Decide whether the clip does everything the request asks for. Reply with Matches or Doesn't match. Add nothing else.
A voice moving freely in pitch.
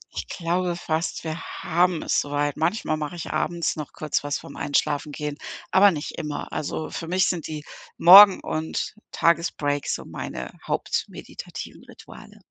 Doesn't match